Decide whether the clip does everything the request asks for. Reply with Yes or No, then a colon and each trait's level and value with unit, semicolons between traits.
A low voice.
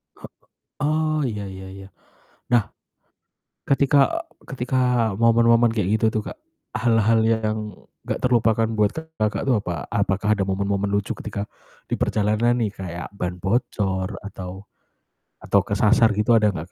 Yes: low, 110 Hz